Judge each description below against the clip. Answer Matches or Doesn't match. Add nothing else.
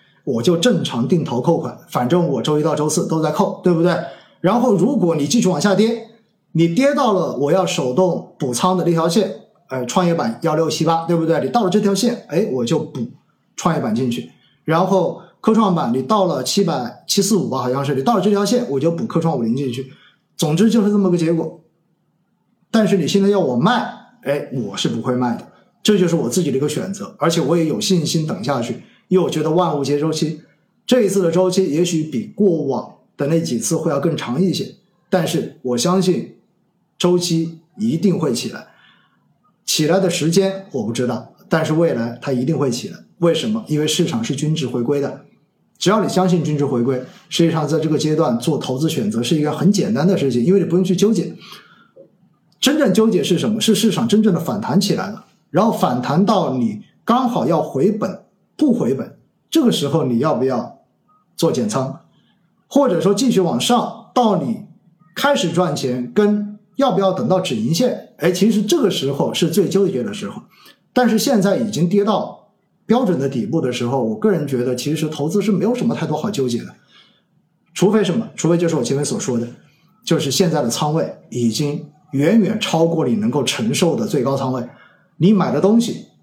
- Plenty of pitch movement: Doesn't match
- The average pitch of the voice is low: Doesn't match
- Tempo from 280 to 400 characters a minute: Matches